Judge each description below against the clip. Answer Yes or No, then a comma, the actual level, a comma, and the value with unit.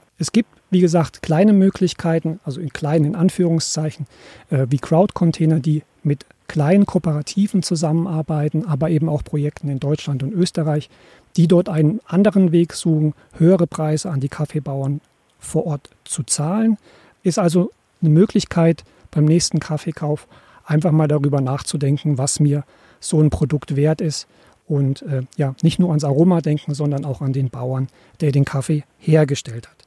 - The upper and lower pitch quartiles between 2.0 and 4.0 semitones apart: Yes, average, 2.9 semitones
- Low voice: No, medium, 155 Hz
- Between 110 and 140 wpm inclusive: No, average, 155 wpm